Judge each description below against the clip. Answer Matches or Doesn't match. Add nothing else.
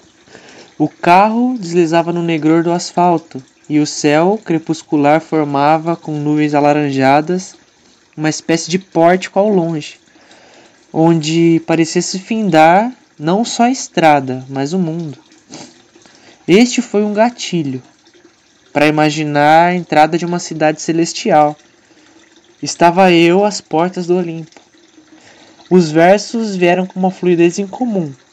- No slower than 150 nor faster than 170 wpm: Doesn't match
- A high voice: Doesn't match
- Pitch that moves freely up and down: Doesn't match